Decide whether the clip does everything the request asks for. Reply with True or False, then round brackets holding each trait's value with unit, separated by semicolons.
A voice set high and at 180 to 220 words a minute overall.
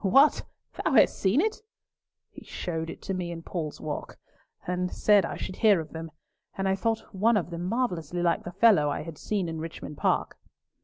False (180 Hz; 200 wpm)